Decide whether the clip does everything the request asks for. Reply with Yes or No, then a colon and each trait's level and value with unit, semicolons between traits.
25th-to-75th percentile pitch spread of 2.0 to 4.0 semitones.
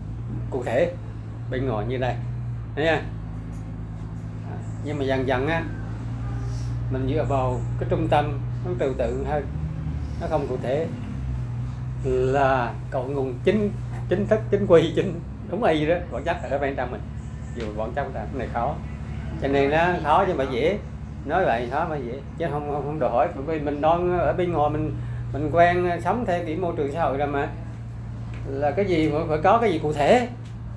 Yes: average, 3.7 semitones